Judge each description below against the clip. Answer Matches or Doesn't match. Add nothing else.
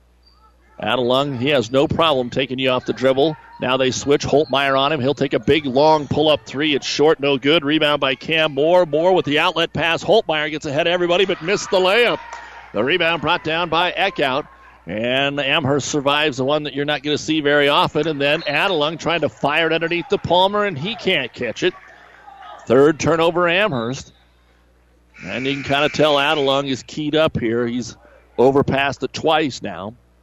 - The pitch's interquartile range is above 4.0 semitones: Doesn't match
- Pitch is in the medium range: Matches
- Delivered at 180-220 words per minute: Matches